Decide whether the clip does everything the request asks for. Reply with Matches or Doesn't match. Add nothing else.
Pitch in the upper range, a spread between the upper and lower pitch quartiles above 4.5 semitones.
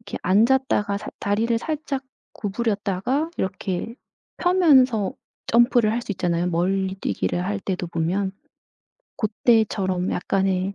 Doesn't match